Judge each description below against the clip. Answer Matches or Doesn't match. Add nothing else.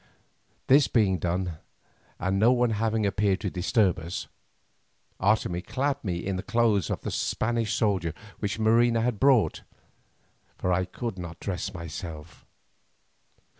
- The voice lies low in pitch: Matches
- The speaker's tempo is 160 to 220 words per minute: Doesn't match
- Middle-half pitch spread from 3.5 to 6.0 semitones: Matches